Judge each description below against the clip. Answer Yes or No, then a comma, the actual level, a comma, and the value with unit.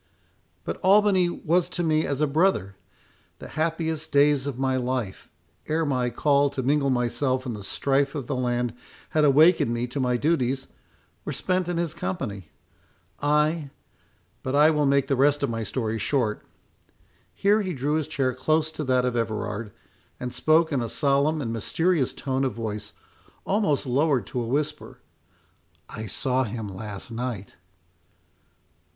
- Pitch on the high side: No, low, 135 Hz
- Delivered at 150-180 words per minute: Yes, average, 155 wpm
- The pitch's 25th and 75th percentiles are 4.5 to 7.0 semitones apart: No, average, 4.1 semitones